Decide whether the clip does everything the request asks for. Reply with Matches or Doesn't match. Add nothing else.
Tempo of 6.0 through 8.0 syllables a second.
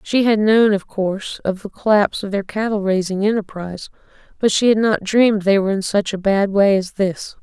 Doesn't match